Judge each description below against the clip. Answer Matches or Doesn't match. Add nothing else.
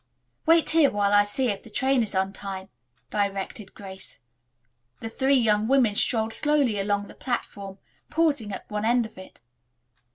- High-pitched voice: Matches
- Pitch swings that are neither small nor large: Matches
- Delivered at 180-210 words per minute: Doesn't match